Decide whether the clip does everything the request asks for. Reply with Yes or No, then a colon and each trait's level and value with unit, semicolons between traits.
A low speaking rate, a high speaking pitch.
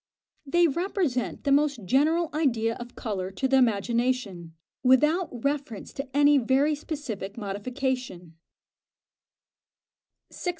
Yes: slow, 110 wpm; very high, 260 Hz